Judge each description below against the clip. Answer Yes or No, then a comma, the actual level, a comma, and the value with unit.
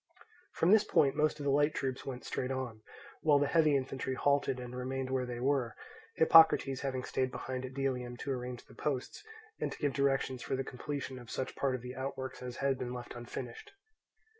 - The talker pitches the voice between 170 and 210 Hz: No, low, 130 Hz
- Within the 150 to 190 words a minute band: No, fast, 205 wpm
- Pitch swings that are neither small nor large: No, narrow, 1.7 semitones